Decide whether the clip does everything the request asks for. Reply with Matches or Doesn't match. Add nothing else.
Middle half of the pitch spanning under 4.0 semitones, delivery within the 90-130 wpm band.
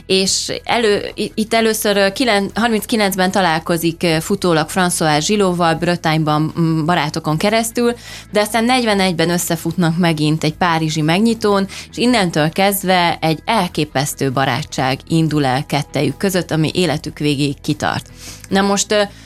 Doesn't match